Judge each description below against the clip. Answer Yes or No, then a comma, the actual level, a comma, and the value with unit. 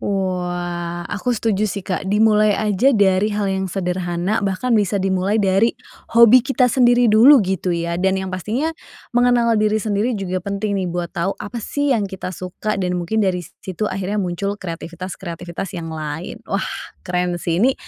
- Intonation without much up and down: No, average, 3.1 semitones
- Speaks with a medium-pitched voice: No, high, 195 Hz